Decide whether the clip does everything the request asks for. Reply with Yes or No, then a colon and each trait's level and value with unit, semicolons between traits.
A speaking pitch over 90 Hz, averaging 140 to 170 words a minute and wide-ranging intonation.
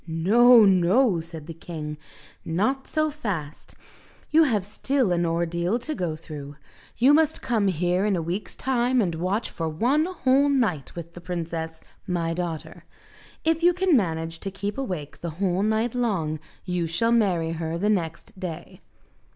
Yes: medium, 185 Hz; average, 160 wpm; wide, 6.4 semitones